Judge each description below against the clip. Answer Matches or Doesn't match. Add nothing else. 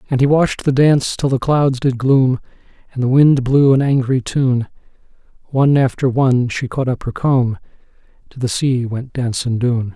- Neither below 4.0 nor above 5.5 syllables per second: Matches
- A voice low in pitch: Matches